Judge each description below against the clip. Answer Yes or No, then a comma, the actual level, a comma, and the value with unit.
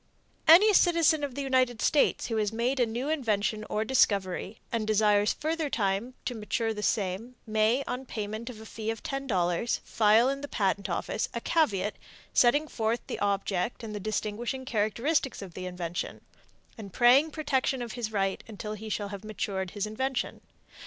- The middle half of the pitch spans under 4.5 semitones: Yes, average, 4.0 semitones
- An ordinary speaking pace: Yes, average, 175 wpm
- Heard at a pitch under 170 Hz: No, high, 220 Hz